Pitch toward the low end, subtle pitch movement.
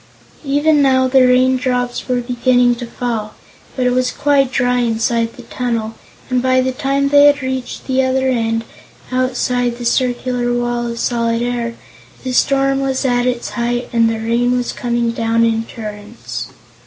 No: high, 245 Hz; narrow, 1.6 semitones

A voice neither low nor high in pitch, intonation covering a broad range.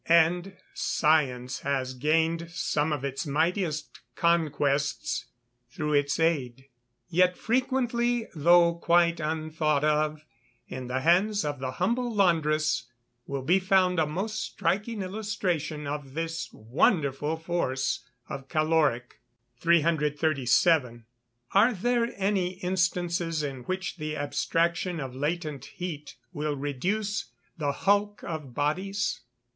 No: medium, 160 Hz; average, 3.9 semitones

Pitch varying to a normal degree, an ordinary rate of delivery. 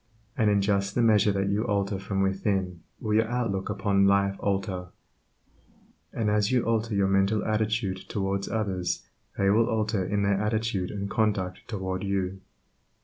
No: narrow, 1.8 semitones; average, 160 wpm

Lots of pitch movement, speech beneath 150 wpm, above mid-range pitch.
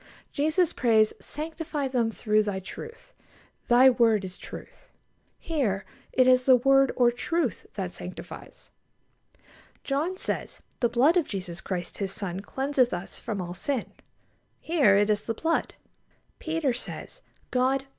Yes: wide, 5.7 semitones; average, 140 wpm; high, 245 Hz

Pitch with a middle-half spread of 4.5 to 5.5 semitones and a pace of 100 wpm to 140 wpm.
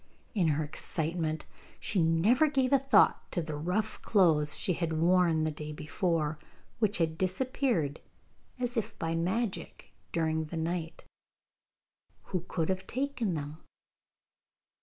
Yes: average, 5.1 semitones; slow, 135 wpm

